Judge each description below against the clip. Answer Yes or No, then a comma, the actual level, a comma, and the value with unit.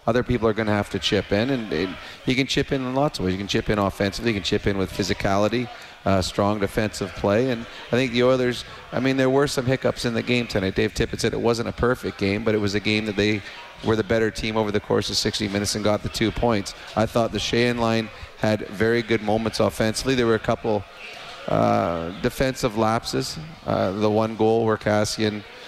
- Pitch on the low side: Yes, low, 110 Hz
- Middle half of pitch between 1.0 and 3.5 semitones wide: Yes, narrow, 2.6 semitones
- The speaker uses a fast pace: Yes, fast, 240 wpm